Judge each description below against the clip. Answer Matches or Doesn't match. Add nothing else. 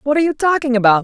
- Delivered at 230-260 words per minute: Doesn't match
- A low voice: Doesn't match